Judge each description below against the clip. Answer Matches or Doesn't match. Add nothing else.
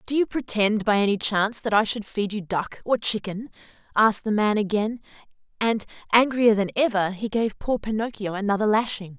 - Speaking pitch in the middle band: Doesn't match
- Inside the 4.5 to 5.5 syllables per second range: Matches